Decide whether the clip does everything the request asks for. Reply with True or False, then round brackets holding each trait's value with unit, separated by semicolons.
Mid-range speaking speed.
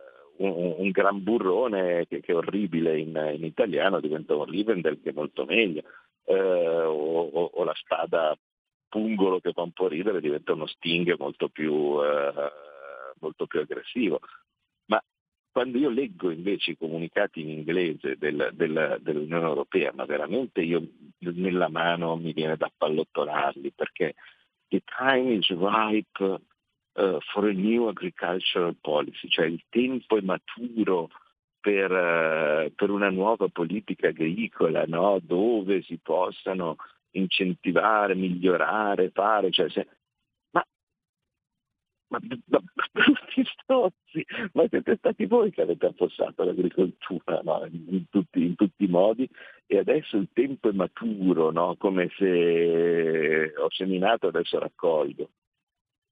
True (135 wpm)